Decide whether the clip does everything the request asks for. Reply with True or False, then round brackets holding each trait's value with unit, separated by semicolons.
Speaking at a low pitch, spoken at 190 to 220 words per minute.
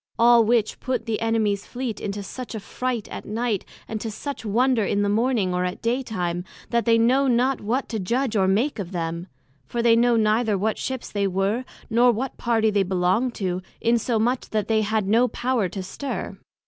False (225 Hz; 200 wpm)